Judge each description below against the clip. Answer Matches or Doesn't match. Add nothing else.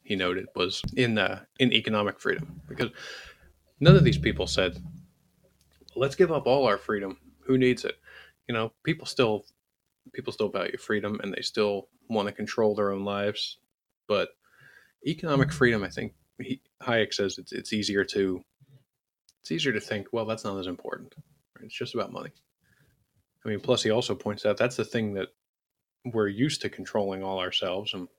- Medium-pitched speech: Doesn't match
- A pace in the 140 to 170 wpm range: Doesn't match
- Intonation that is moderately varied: Matches